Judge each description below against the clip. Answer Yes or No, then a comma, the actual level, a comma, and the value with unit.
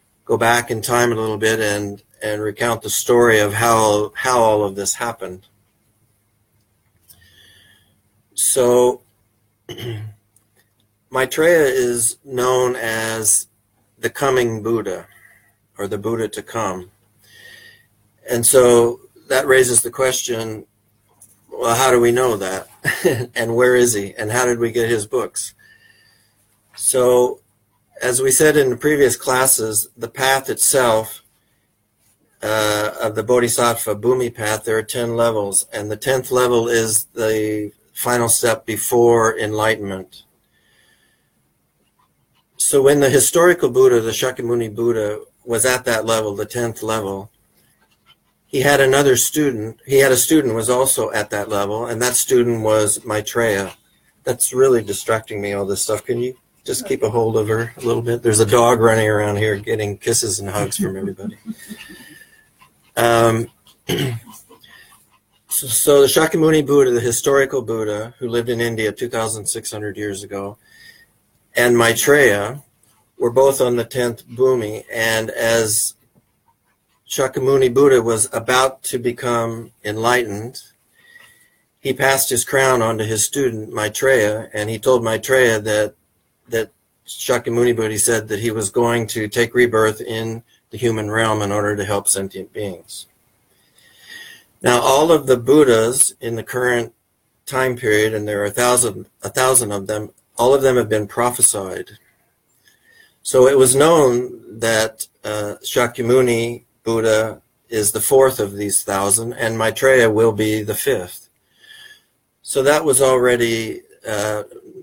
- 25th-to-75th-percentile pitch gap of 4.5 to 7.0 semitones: No, average, 2.8 semitones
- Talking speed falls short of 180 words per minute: Yes, average, 140 wpm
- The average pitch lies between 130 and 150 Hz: No, low, 115 Hz